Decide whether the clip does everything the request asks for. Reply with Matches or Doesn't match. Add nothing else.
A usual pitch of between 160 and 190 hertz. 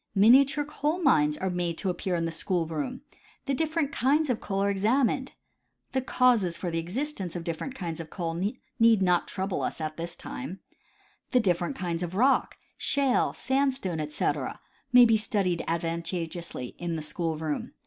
Matches